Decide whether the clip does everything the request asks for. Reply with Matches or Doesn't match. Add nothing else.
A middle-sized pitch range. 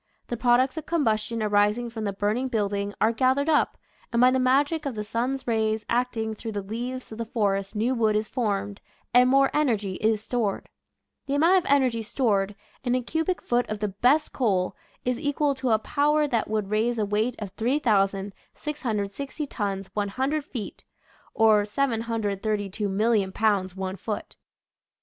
Matches